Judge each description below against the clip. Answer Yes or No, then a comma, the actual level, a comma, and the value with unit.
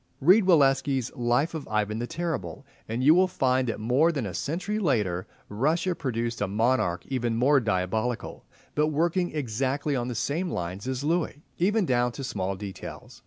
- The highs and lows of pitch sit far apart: Yes, wide, 5.7 semitones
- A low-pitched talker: Yes, low, 130 Hz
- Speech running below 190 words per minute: Yes, average, 170 wpm